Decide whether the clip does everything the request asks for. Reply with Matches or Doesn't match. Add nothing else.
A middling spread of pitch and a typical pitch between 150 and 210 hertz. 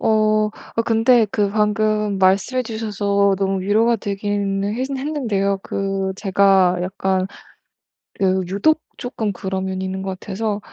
Doesn't match